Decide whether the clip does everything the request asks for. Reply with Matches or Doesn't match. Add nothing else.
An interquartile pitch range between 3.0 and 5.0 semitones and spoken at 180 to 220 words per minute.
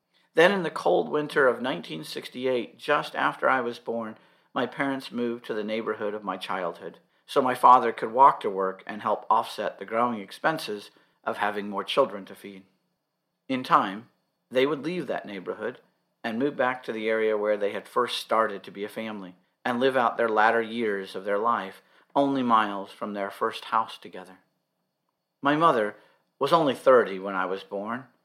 Matches